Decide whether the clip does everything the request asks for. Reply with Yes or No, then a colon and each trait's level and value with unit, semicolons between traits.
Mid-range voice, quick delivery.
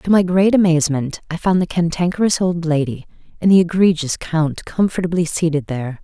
No: medium, 170 Hz; average, 170 wpm